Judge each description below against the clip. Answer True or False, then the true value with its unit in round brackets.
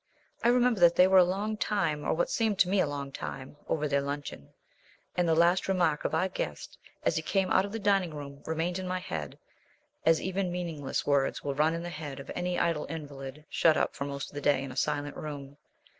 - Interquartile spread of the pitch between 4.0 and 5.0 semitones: True (4.3 semitones)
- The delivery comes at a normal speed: False (235 wpm)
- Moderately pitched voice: True (160 Hz)